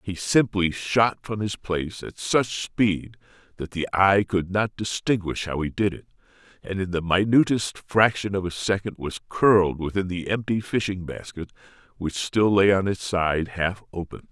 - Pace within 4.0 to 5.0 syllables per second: Yes, 4.5 syllables/s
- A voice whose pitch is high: No, very low, 95 Hz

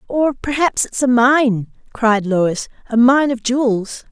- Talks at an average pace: Yes, average, 145 wpm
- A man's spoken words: No, female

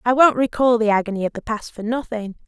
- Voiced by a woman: Yes, female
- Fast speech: Yes, fast, 240 wpm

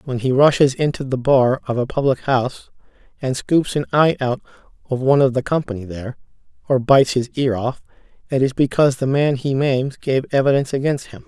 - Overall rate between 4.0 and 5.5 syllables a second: No, 5.8 syllables/s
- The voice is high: No, low, 130 Hz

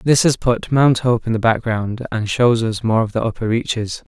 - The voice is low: Yes, low, 115 Hz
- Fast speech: Yes, fast, 230 wpm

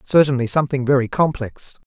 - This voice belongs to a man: Yes, male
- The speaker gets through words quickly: No, slow, 130 wpm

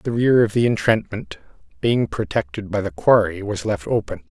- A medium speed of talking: Yes, average, 180 wpm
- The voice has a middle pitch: No, low, 110 Hz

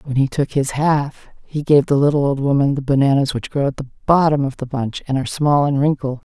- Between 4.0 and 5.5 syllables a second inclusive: No, 5.8 syllables/s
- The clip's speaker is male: No, female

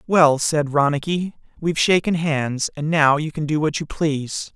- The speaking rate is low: No, average, 185 wpm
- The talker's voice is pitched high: No, medium, 155 Hz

